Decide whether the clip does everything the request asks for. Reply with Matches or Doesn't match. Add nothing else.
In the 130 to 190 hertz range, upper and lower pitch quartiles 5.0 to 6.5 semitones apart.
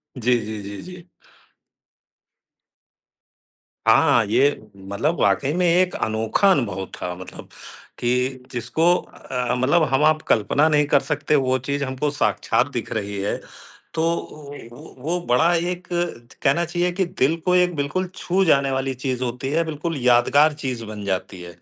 Matches